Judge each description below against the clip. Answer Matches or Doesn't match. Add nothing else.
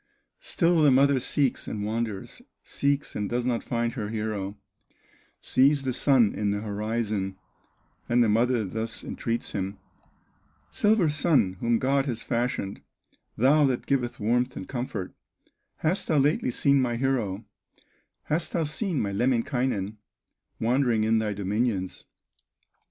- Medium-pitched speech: Doesn't match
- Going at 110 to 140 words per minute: Matches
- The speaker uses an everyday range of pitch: Matches